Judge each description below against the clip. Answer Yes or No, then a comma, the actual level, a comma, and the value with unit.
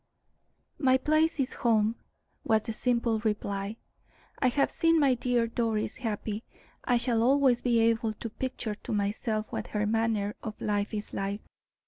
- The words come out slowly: No, average, 155 wpm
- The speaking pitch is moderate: No, high, 225 Hz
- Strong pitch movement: No, average, 2.7 semitones